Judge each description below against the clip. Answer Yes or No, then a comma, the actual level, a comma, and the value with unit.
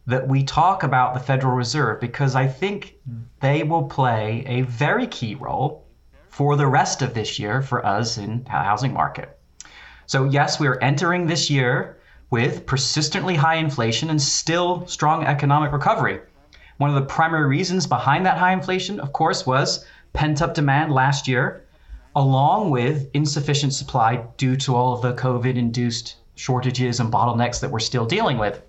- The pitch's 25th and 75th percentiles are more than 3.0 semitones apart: Yes, average, 3.4 semitones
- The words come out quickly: No, average, 170 wpm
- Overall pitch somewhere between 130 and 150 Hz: Yes, low, 135 Hz